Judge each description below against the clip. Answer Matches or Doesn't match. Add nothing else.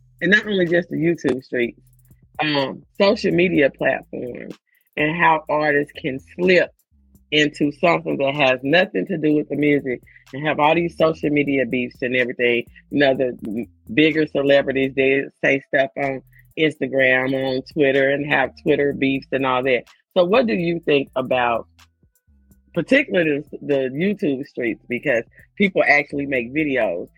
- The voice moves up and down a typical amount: Matches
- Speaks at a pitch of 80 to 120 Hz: Doesn't match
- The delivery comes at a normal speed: Matches